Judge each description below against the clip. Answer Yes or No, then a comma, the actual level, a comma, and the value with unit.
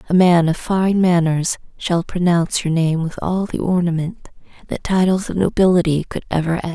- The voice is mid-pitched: Yes, medium, 175 Hz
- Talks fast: No, average, 180 wpm